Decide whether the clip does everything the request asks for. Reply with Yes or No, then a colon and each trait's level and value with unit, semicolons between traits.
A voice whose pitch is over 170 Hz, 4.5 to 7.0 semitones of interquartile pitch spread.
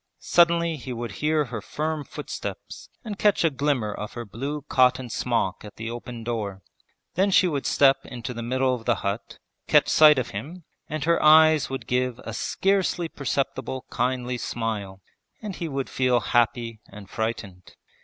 No: low, 125 Hz; average, 5.0 semitones